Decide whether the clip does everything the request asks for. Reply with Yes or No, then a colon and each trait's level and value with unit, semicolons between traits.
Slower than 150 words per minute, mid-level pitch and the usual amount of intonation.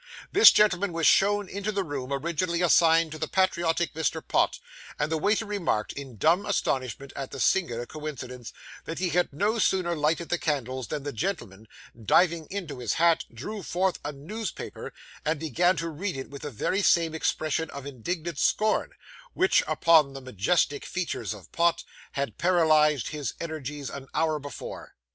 No: average, 170 wpm; medium, 160 Hz; average, 4.2 semitones